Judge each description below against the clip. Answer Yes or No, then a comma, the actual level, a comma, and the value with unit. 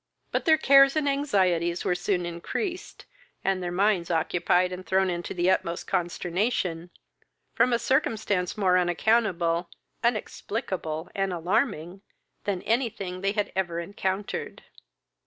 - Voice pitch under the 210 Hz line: Yes, medium, 185 Hz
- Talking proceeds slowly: Yes, slow, 125 wpm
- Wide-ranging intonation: No, average, 3.6 semitones